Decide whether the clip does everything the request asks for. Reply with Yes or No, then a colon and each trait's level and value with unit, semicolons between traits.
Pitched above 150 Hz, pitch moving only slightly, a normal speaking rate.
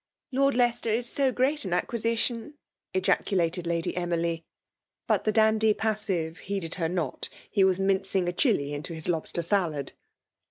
No: high, 190 Hz; average, 4.8 semitones; average, 175 wpm